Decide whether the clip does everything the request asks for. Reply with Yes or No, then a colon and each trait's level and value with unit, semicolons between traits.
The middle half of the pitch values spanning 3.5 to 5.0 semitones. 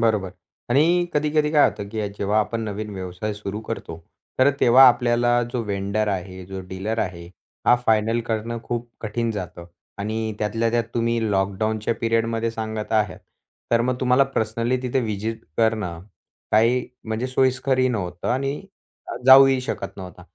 No: average, 2.8 semitones